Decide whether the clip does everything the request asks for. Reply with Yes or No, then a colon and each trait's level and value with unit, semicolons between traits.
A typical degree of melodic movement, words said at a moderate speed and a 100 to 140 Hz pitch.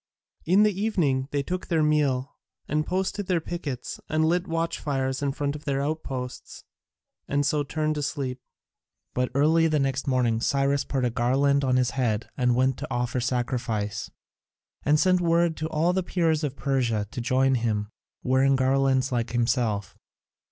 Yes: average, 3.6 semitones; average, 175 wpm; low, 135 Hz